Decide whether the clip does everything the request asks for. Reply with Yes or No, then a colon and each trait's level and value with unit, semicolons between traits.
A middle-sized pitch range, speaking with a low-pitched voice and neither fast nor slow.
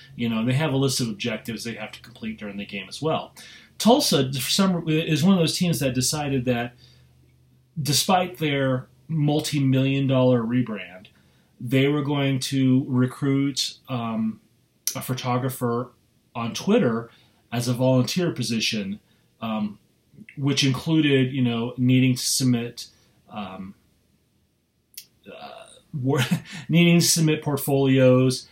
No: average, 3.5 semitones; low, 130 Hz; slow, 125 wpm